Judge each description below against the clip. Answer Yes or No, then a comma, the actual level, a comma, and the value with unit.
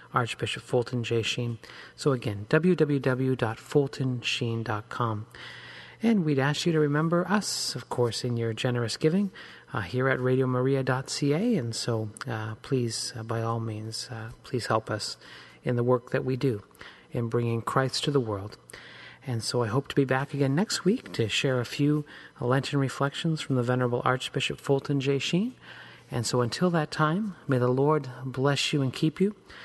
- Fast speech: No, average, 170 wpm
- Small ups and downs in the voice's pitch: No, average, 3.4 semitones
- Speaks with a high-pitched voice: No, low, 130 Hz